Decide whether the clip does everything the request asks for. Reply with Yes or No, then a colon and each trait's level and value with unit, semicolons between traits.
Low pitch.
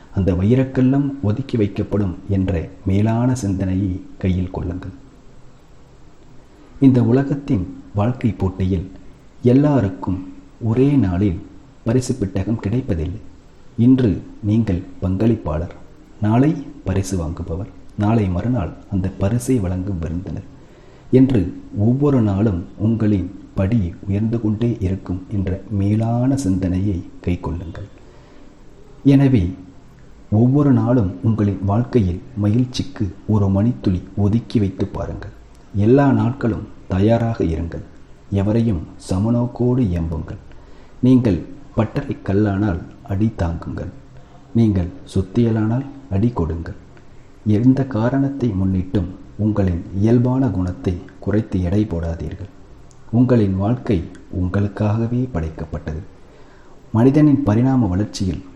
Yes: low, 100 Hz